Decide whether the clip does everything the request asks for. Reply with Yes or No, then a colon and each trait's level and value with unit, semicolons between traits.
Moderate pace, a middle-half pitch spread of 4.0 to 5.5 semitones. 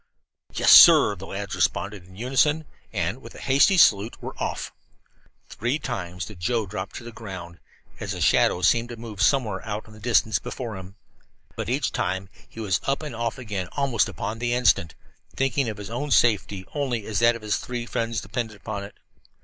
No: average, 195 wpm; average, 3.6 semitones